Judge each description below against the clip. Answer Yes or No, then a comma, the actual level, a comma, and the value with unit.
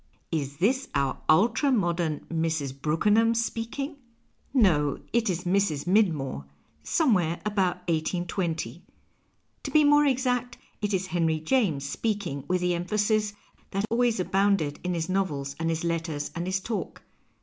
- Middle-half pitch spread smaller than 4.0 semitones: No, wide, 5.4 semitones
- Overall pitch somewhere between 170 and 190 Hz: Yes, medium, 185 Hz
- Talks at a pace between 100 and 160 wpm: Yes, average, 140 wpm